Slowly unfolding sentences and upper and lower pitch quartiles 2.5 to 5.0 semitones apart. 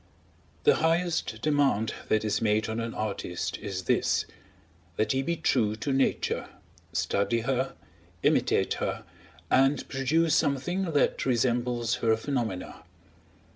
Yes: slow, 125 wpm; average, 4.7 semitones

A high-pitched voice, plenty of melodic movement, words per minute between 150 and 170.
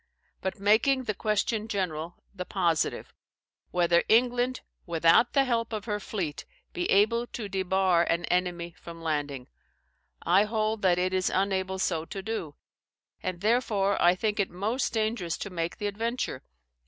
No: high, 195 Hz; average, 3.9 semitones; average, 155 wpm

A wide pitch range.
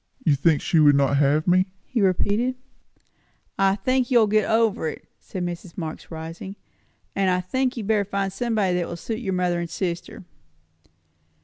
No: average, 4.1 semitones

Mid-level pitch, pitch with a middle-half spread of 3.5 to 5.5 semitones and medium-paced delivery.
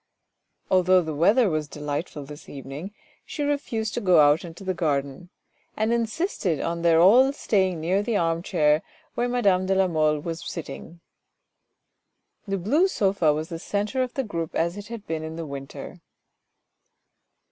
Yes: medium, 175 Hz; average, 4.8 semitones; average, 170 wpm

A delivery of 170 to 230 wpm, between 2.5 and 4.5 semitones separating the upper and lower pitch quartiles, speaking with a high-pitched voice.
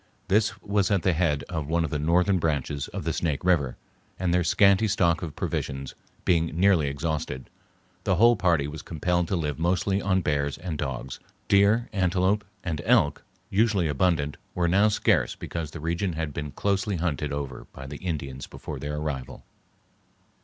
No: average, 175 wpm; average, 4.2 semitones; very low, 85 Hz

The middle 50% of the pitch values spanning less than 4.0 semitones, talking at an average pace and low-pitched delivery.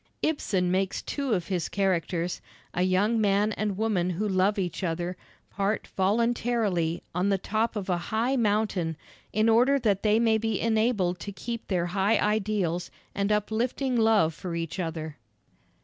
No: average, 3.5 semitones; average, 160 wpm; high, 200 Hz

